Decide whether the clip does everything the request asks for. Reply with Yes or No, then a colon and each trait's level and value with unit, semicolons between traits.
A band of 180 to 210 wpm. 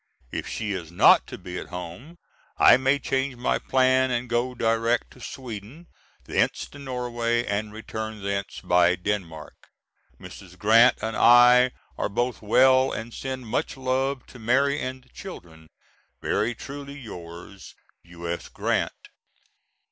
No: average, 140 wpm